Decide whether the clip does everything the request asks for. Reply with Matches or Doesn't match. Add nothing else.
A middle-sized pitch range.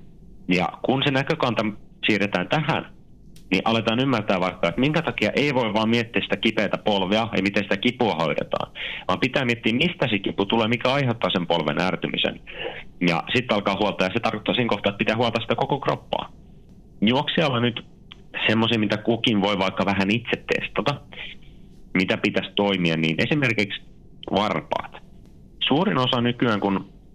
Matches